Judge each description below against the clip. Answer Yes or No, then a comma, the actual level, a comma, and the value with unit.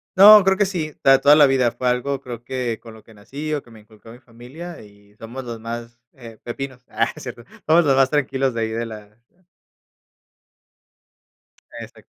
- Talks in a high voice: No, low, 125 Hz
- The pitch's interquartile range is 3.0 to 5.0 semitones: Yes, average, 3.5 semitones